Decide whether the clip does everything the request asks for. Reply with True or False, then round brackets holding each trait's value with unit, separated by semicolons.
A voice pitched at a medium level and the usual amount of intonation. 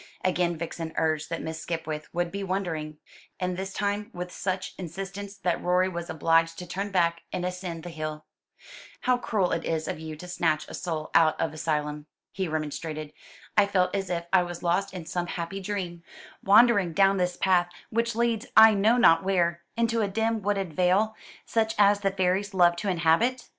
True (180 Hz; 3.2 semitones)